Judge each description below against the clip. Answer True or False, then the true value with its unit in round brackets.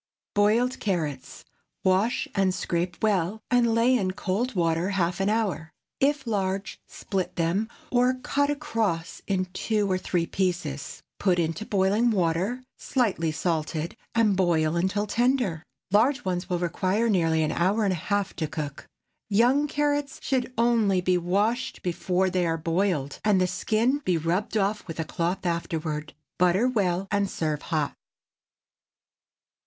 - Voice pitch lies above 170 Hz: True (190 Hz)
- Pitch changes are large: False (4.5 semitones)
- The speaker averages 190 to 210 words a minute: False (150 wpm)